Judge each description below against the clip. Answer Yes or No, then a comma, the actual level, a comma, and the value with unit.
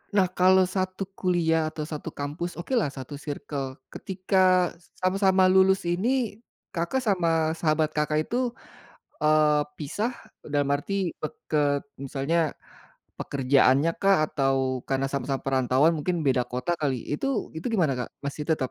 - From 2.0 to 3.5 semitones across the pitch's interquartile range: No, average, 4.6 semitones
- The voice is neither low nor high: Yes, medium, 155 Hz